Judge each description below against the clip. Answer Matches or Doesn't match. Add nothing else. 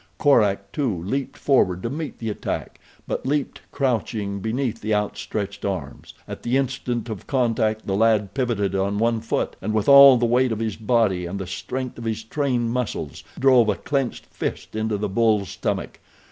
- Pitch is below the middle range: Matches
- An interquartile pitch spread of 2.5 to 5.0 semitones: Matches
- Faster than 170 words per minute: Matches